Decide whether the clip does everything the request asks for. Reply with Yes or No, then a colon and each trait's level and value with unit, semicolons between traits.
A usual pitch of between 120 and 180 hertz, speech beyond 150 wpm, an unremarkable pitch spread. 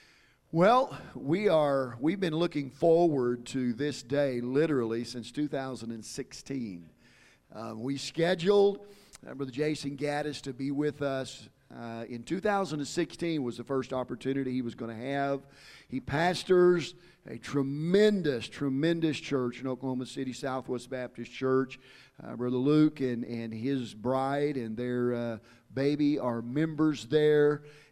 No: low, 135 Hz; slow, 135 wpm; average, 3.6 semitones